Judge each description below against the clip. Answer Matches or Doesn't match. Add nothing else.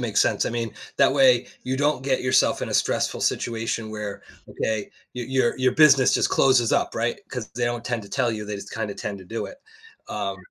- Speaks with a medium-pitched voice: Doesn't match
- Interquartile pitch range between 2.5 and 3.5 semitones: Matches